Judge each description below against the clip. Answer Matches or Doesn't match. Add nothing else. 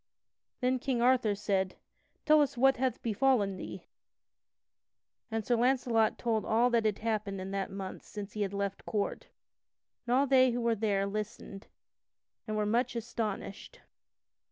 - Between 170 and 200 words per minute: Doesn't match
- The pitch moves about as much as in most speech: Matches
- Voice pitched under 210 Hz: Doesn't match